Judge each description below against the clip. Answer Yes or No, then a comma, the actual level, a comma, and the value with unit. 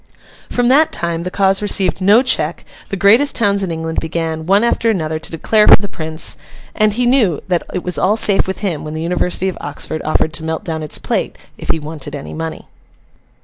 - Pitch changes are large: No, average, 4.2 semitones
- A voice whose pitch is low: No, medium, 180 Hz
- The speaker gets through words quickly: Yes, fast, 215 wpm